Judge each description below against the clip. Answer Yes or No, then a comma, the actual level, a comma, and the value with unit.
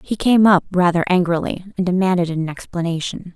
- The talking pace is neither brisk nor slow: Yes, average, 160 wpm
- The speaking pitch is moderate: Yes, medium, 180 Hz